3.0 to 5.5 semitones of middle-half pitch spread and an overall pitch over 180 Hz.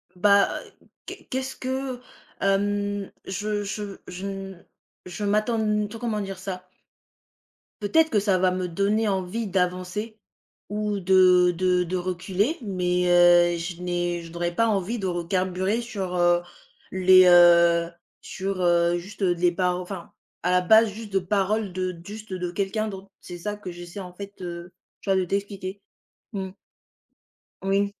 No: narrow, 2.4 semitones; high, 190 Hz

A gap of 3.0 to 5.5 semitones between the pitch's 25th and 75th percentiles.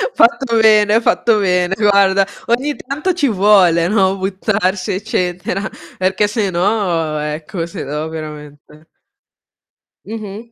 Yes: average, 3.8 semitones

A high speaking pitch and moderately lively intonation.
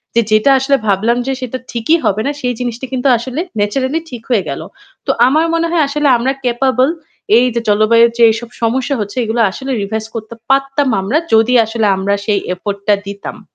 Yes: high, 235 Hz; average, 3.6 semitones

